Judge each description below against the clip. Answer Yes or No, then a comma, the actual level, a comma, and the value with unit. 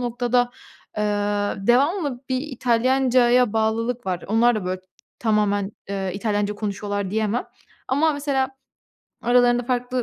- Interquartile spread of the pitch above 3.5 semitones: No, average, 3.2 semitones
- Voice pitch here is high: Yes, high, 240 Hz